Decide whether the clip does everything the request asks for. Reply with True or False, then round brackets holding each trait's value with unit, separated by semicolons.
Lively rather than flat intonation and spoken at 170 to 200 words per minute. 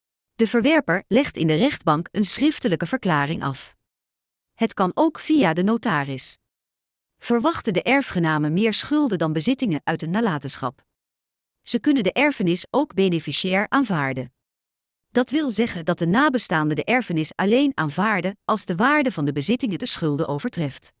False (8.4 semitones; 150 wpm)